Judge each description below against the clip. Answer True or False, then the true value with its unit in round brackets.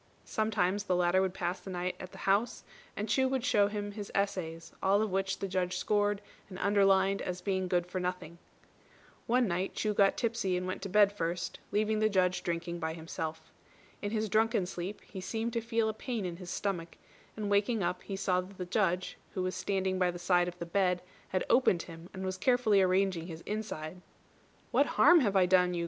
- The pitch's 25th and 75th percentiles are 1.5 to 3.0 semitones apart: True (2.5 semitones)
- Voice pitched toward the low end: False (190 Hz)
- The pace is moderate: False (210 wpm)